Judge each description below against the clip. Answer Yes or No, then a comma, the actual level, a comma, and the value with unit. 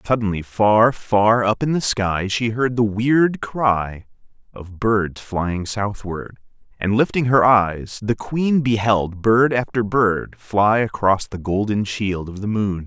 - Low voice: Yes, low, 110 Hz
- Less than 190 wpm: Yes, average, 160 wpm